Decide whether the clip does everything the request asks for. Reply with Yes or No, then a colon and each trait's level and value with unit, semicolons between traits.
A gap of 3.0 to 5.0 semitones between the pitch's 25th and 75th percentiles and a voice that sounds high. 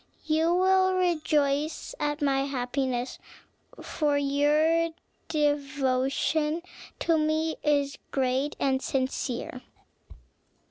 No: narrow, 2.5 semitones; very high, 290 Hz